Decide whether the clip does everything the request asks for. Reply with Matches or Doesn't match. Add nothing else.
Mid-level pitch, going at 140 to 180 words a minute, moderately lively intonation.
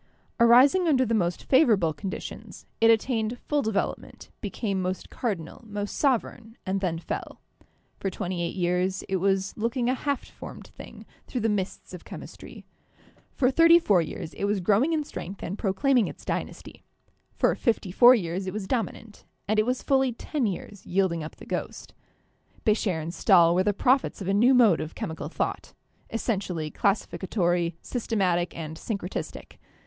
Doesn't match